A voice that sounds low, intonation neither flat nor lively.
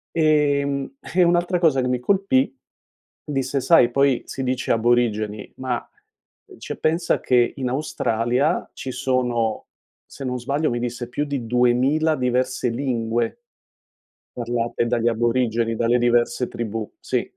Yes: low, 125 Hz; average, 3.0 semitones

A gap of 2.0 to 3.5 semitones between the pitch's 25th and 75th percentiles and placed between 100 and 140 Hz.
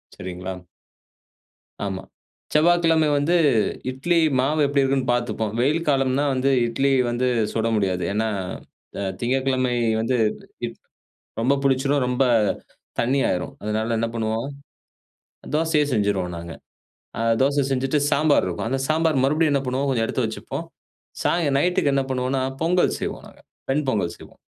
No: average, 4.1 semitones; low, 135 Hz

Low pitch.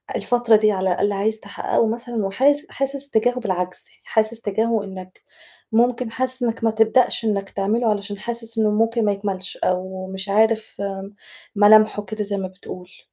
No: high, 215 Hz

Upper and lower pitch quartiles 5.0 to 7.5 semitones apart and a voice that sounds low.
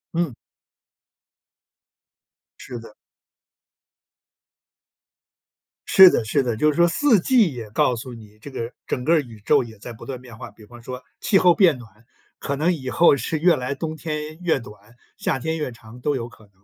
Yes: wide, 5.6 semitones; low, 130 Hz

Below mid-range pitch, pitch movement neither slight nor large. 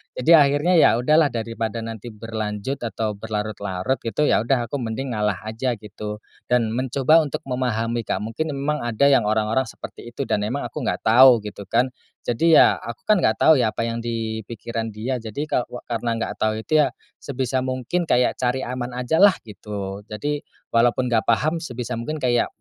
Yes: low, 120 Hz; average, 3.2 semitones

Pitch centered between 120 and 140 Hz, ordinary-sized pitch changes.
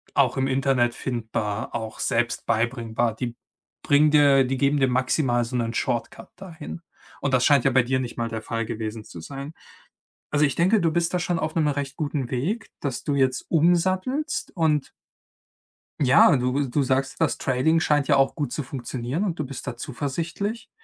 Yes: low, 135 Hz; average, 4.1 semitones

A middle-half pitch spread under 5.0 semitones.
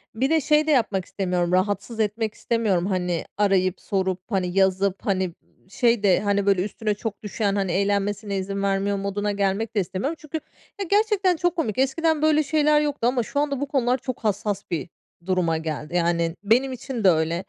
No: wide, 5.6 semitones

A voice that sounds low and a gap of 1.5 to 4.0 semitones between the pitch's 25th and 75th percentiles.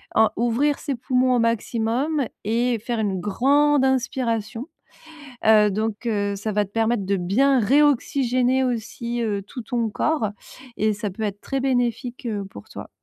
No: high, 235 Hz; average, 3.5 semitones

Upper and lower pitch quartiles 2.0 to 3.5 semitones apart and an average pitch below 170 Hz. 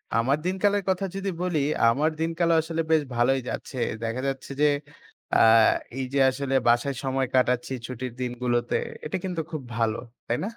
No: average, 4.9 semitones; low, 135 Hz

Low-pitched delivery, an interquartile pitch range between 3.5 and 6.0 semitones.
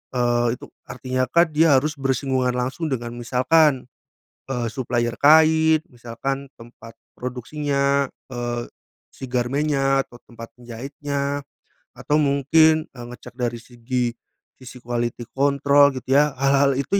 No: low, 130 Hz; average, 2.8 semitones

